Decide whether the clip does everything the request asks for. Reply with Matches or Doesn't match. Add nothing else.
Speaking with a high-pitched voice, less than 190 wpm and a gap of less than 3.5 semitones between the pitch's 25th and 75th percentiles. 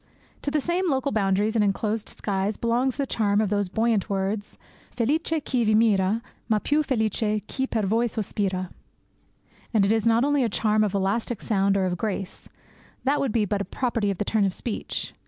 Doesn't match